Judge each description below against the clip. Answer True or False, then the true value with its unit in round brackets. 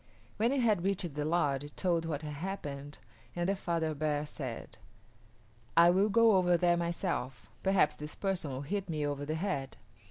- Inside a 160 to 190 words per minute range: True (185 wpm)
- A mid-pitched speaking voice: True (170 Hz)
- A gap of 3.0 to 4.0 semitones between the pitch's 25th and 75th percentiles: False (4.5 semitones)